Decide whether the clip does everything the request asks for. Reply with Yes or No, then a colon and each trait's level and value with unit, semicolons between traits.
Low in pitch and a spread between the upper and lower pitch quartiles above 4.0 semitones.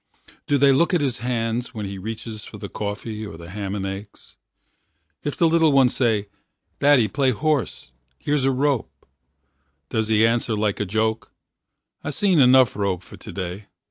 Yes: low, 115 Hz; average, 4.9 semitones